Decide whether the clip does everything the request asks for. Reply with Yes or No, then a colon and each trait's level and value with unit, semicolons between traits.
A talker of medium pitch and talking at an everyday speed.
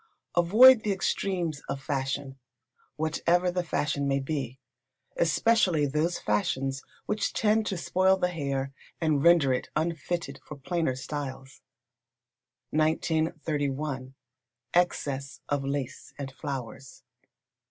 No: medium, 150 Hz; slow, 110 wpm